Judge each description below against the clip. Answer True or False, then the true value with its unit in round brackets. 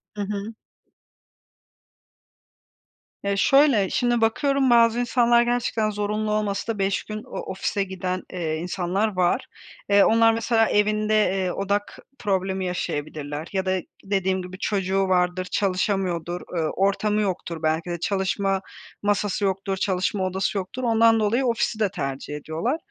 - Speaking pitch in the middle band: False (195 Hz)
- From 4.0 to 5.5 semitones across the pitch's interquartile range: False (2.7 semitones)